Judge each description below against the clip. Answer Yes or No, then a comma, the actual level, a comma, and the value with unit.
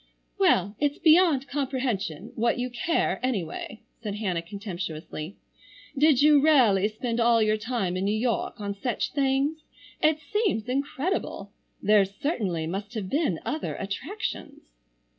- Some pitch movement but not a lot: No, wide, 6.0 semitones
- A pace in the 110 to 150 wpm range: Yes, slow, 135 wpm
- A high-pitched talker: Yes, high, 230 Hz